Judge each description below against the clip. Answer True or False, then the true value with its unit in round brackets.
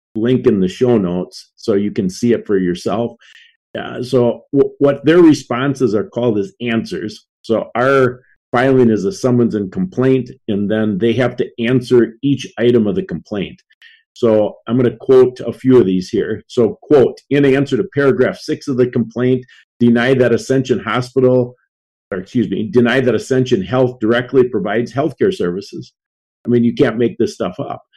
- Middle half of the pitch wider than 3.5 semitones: False (2.7 semitones)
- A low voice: True (125 Hz)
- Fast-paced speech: False (180 wpm)